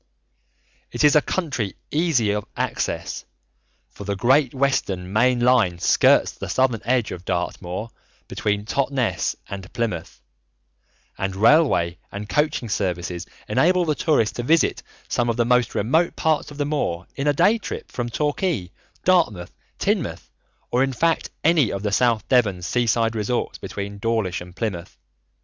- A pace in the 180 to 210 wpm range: No, average, 150 wpm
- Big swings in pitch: Yes, wide, 6.1 semitones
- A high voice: No, low, 120 Hz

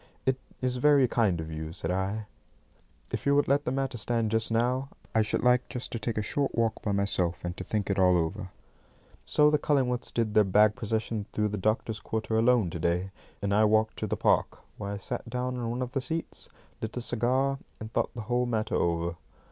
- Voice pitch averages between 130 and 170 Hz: No, low, 110 Hz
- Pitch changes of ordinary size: Yes, average, 3.7 semitones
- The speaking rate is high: Yes, fast, 220 wpm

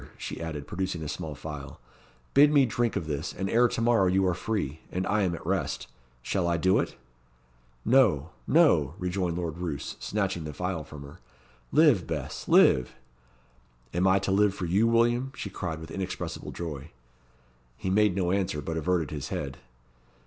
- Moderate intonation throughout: Yes, average, 4.1 semitones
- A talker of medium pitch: No, very low, 90 Hz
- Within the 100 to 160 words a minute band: No, average, 180 wpm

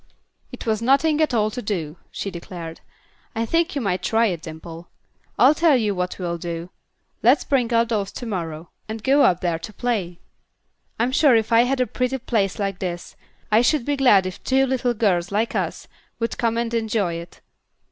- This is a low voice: No, high, 220 Hz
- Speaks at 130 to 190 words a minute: No, average, 200 wpm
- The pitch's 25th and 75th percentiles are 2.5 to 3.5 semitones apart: No, wide, 5.5 semitones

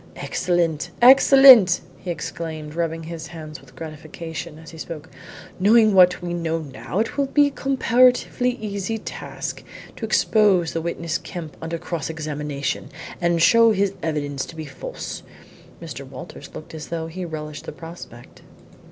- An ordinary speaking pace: Yes, average, 150 wpm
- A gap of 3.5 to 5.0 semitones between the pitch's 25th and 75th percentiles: Yes, average, 4.3 semitones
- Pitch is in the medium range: Yes, medium, 165 Hz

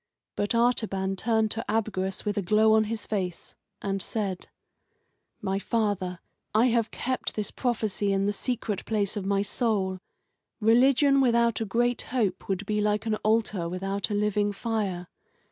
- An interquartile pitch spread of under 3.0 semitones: Yes, narrow, 2.6 semitones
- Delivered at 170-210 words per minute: No, average, 160 wpm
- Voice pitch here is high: Yes, high, 210 Hz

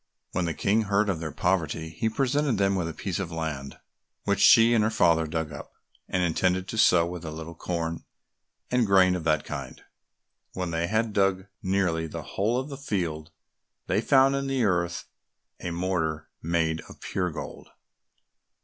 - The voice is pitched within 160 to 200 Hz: No, very low, 90 Hz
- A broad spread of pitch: No, average, 4.1 semitones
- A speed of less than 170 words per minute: No, average, 180 wpm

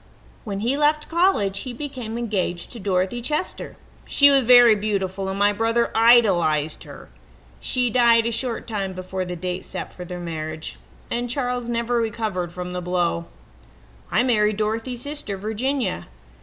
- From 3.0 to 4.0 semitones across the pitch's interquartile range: No, average, 4.7 semitones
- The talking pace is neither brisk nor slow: Yes, average, 155 wpm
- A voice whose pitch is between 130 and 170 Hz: No, high, 220 Hz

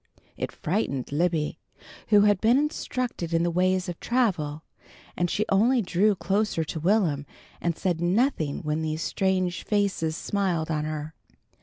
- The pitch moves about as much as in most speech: Yes, average, 4.5 semitones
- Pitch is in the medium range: Yes, medium, 180 Hz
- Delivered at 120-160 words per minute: Yes, average, 150 wpm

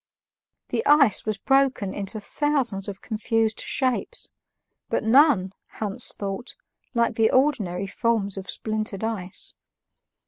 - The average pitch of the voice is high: Yes, high, 220 Hz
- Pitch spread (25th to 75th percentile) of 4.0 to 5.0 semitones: Yes, average, 4.4 semitones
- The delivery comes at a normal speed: No, slow, 115 wpm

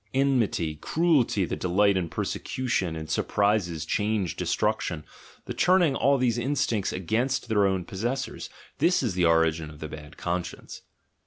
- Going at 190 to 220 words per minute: No, average, 160 wpm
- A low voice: Yes, low, 100 Hz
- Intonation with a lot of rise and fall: Yes, wide, 7.0 semitones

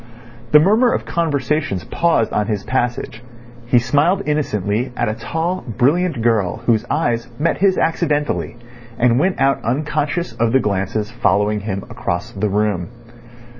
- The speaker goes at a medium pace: Yes, average, 145 wpm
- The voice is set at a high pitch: No, low, 120 Hz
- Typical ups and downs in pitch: No, wide, 6.2 semitones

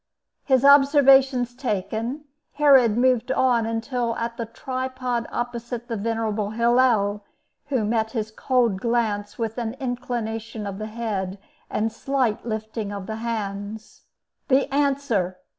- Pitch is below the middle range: No, high, 230 Hz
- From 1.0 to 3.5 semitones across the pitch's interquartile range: Yes, average, 2.8 semitones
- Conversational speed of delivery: No, slow, 130 wpm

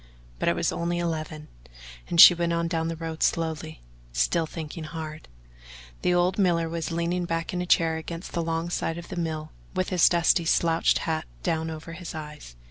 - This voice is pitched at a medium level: Yes, medium, 165 Hz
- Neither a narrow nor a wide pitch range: No, narrow, 1.3 semitones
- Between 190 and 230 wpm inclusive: Yes, average, 195 wpm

